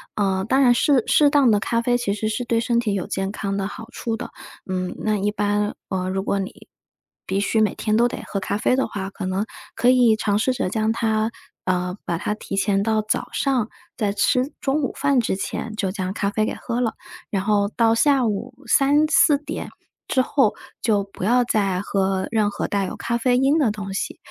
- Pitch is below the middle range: No, high, 215 Hz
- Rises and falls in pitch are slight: No, average, 3.6 semitones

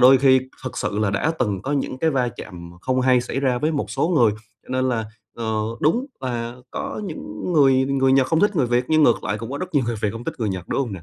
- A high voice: No, low, 130 Hz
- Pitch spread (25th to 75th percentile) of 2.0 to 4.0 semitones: Yes, average, 3.4 semitones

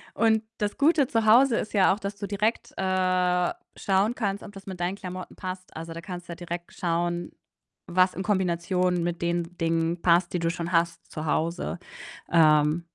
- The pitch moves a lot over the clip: No, narrow, 2.6 semitones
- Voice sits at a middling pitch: Yes, medium, 180 Hz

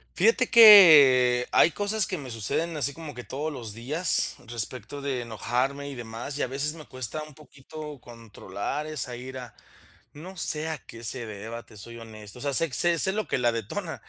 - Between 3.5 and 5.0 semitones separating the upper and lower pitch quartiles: Yes, average, 4.7 semitones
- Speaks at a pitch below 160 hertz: Yes, low, 135 Hz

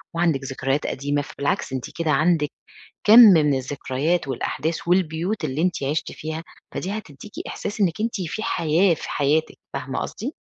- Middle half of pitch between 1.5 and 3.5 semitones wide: No, average, 3.9 semitones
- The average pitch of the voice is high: No, medium, 160 Hz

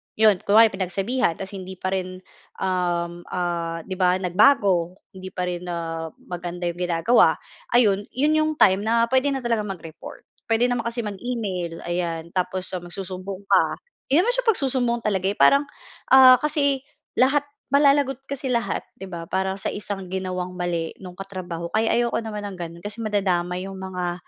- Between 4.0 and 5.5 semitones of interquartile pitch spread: Yes, average, 4.7 semitones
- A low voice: No, high, 190 Hz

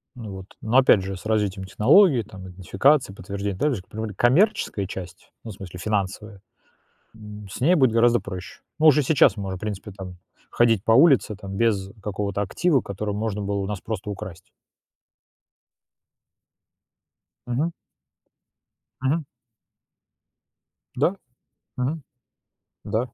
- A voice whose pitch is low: Yes, low, 105 Hz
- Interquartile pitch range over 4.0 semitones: Yes, average, 4.4 semitones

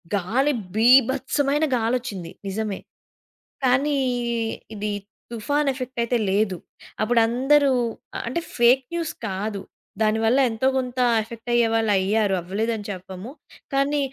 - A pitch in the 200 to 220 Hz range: No, high, 230 Hz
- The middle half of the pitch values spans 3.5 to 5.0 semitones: Yes, average, 3.8 semitones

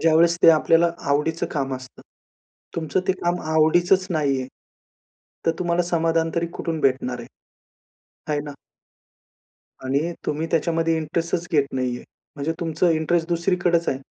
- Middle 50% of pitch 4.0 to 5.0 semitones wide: No, average, 2.7 semitones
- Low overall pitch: No, medium, 165 Hz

